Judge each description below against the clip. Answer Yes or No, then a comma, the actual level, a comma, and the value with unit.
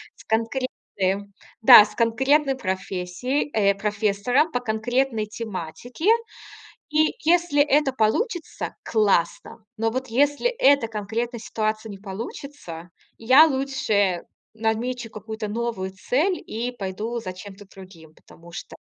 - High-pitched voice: Yes, high, 225 Hz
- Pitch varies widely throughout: No, average, 4.5 semitones